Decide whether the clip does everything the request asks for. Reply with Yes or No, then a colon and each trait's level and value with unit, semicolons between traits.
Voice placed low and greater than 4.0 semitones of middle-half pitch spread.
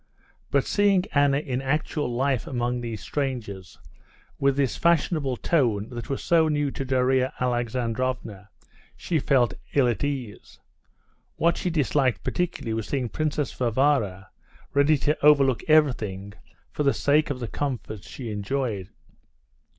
No: low, 130 Hz; average, 3.6 semitones